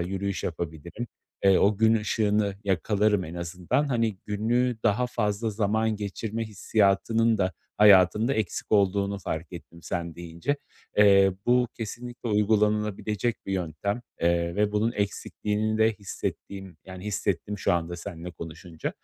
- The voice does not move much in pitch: No, average, 3.1 semitones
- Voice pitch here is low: Yes, low, 100 Hz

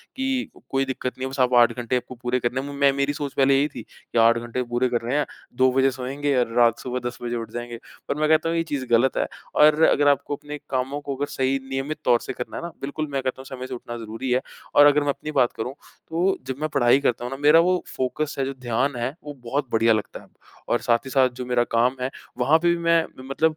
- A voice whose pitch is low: Yes, low, 130 Hz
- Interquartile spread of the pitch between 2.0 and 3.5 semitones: Yes, average, 2.8 semitones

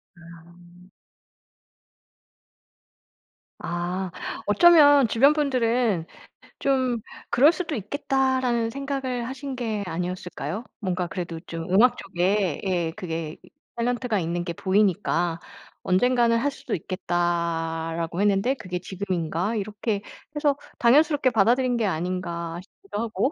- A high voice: Yes, high, 200 Hz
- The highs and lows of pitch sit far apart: Yes, wide, 6.3 semitones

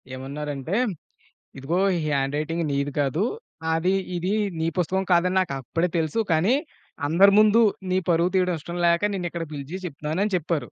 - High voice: No, medium, 170 Hz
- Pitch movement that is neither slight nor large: Yes, average, 3.7 semitones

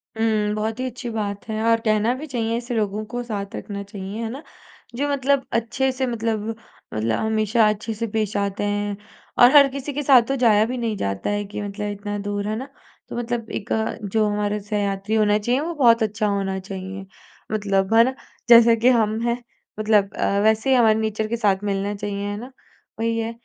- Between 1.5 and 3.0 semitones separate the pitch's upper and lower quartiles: Yes, narrow, 2.4 semitones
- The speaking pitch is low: No, high, 215 Hz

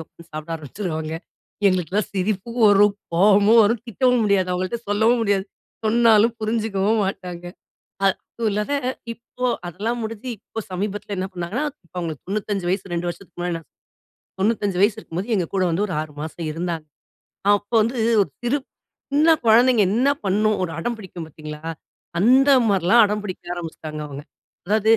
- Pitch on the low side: No, high, 200 Hz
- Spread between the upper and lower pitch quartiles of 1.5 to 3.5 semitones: No, average, 4.0 semitones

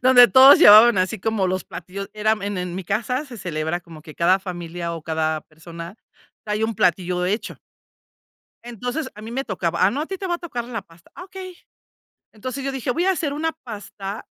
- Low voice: No, high, 210 Hz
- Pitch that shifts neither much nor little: No, wide, 6.1 semitones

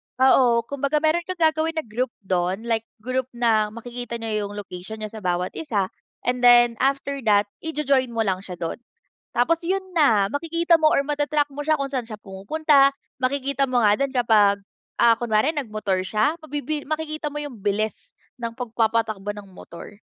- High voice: Yes, high, 245 Hz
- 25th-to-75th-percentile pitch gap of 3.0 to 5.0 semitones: No, wide, 5.4 semitones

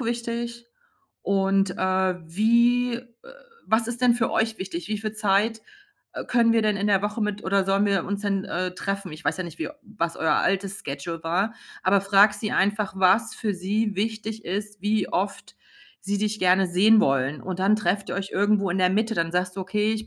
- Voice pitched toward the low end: No, high, 200 Hz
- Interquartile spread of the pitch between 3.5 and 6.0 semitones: No, narrow, 2.6 semitones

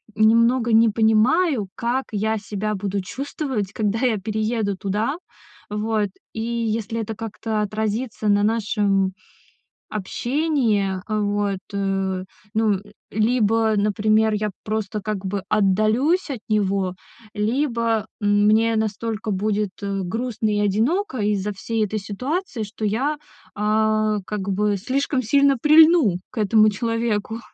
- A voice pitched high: Yes, high, 215 Hz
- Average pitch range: No, narrow, 2.0 semitones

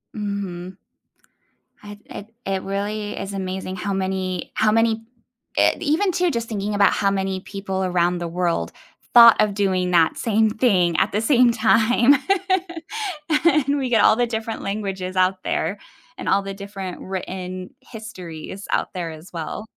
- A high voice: Yes, high, 195 Hz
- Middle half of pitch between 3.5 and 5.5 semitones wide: No, average, 3.0 semitones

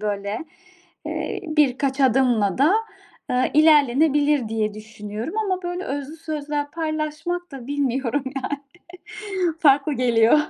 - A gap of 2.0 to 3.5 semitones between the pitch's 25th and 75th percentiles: No, average, 4.2 semitones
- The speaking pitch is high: Yes, very high, 280 Hz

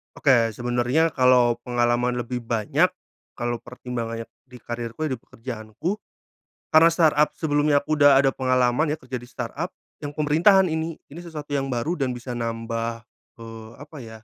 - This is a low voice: Yes, low, 125 Hz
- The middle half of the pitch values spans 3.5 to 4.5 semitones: Yes, average, 4.0 semitones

